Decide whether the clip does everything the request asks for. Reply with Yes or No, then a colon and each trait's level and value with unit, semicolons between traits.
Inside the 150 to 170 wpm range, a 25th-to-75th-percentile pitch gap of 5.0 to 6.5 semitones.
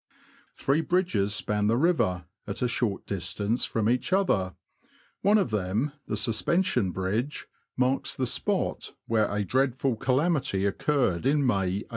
Yes: average, 155 wpm; wide, 5.5 semitones